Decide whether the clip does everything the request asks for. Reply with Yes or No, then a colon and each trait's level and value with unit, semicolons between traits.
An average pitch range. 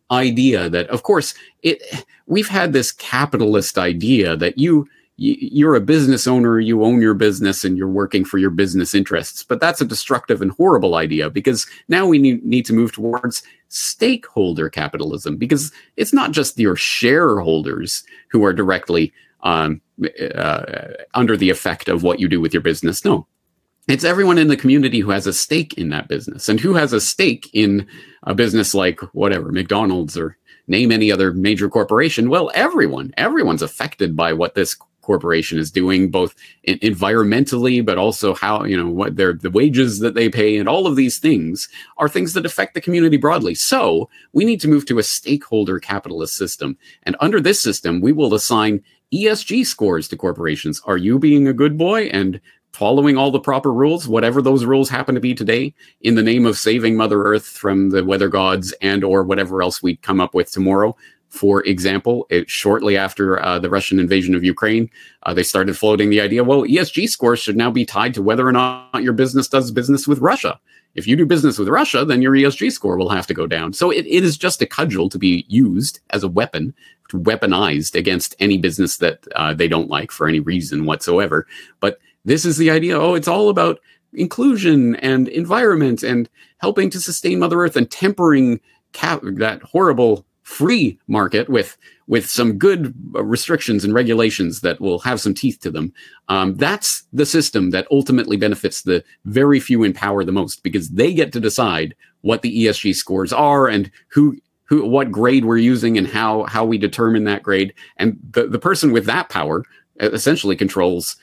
No: wide, 6.0 semitones